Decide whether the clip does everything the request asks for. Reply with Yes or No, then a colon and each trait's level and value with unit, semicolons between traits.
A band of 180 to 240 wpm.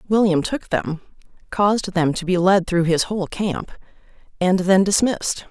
No: average, 165 wpm